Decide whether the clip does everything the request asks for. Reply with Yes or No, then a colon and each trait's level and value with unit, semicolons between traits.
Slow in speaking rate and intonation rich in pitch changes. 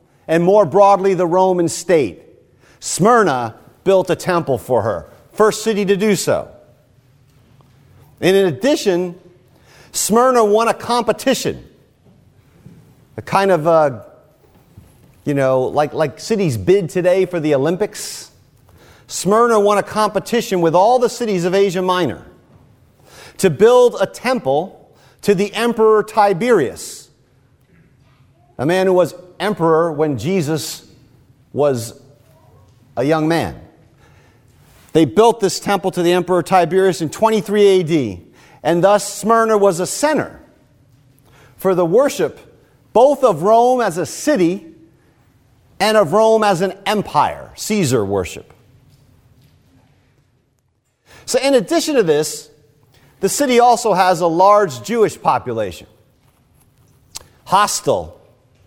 Yes: slow, 120 wpm; wide, 6.9 semitones